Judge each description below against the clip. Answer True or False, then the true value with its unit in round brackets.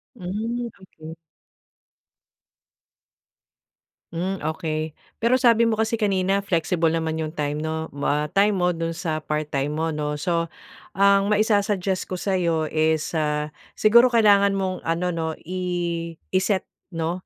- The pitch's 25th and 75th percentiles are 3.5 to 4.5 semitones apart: True (3.8 semitones)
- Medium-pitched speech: True (175 Hz)